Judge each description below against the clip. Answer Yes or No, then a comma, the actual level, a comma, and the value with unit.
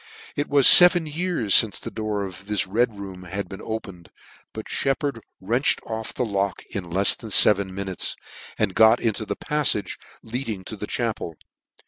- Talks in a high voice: No, low, 110 Hz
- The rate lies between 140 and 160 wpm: No, average, 170 wpm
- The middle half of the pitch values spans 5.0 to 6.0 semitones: No, average, 3.9 semitones